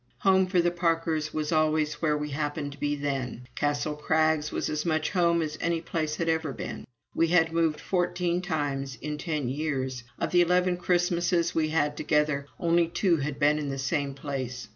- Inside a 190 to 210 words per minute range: Yes, average, 195 wpm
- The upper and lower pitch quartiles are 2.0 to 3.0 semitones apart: Yes, narrow, 2.6 semitones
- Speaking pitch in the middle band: Yes, medium, 155 Hz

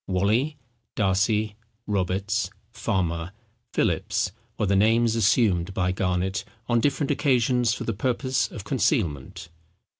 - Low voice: Yes, low, 105 Hz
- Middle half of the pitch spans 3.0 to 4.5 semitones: Yes, average, 4.1 semitones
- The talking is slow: Yes, slow, 115 wpm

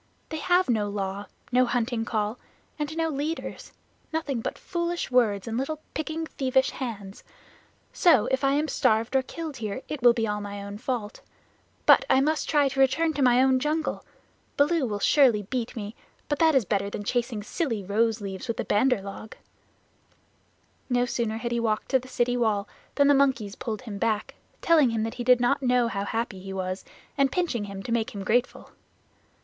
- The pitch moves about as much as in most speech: Yes, average, 4.6 semitones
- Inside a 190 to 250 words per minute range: Yes, average, 195 wpm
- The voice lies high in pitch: Yes, high, 245 Hz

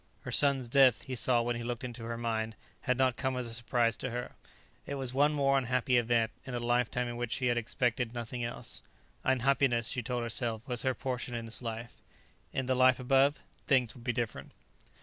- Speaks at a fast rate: Yes, fast, 210 wpm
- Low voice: Yes, low, 120 Hz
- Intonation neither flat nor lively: No, narrow, 1.8 semitones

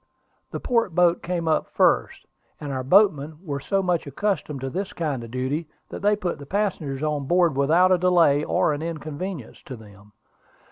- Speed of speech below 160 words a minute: No, average, 175 wpm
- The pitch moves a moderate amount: Yes, average, 4.6 semitones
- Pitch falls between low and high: Yes, medium, 155 Hz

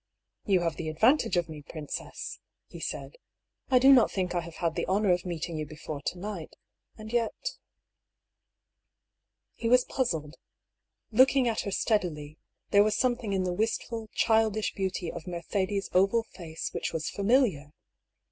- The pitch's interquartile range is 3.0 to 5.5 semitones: Yes, average, 5.2 semitones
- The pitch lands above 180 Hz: Yes, high, 190 Hz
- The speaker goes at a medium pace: Yes, average, 165 wpm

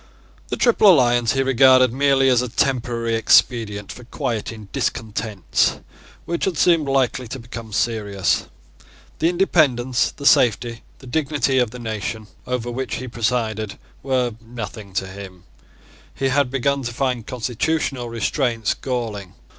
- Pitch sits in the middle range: No, low, 120 Hz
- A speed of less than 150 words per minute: Yes, average, 140 wpm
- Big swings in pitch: No, average, 3.0 semitones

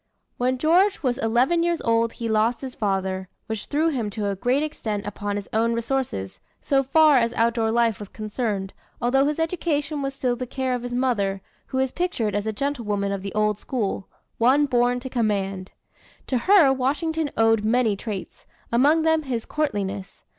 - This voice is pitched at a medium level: No, high, 240 Hz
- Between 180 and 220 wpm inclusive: Yes, average, 185 wpm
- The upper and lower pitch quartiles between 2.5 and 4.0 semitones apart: No, average, 4.5 semitones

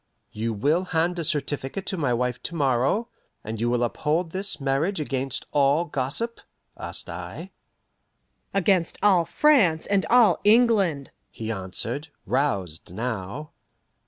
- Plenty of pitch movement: Yes, wide, 6.8 semitones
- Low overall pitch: No, medium, 150 Hz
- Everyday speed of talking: No, slow, 130 wpm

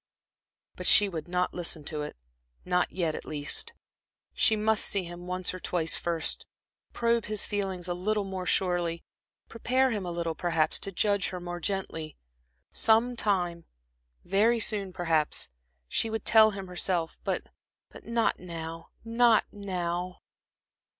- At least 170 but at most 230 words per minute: No, average, 145 wpm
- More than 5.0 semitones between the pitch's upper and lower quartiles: No, average, 3.5 semitones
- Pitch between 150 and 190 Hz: Yes, medium, 185 Hz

